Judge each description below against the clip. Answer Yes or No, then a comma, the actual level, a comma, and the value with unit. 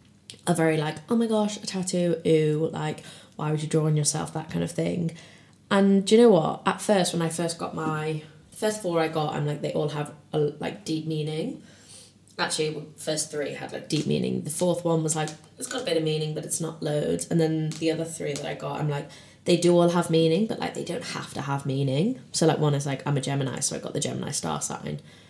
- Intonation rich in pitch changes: No, narrow, 2.5 semitones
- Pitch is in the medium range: Yes, medium, 155 Hz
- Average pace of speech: No, fast, 250 wpm